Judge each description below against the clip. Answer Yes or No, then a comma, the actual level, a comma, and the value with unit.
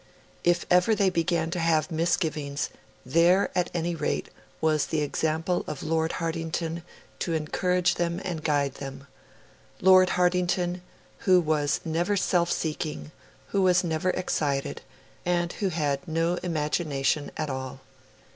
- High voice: No, medium, 165 Hz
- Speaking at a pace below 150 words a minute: Yes, slow, 135 wpm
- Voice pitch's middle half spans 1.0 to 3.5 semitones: Yes, average, 2.7 semitones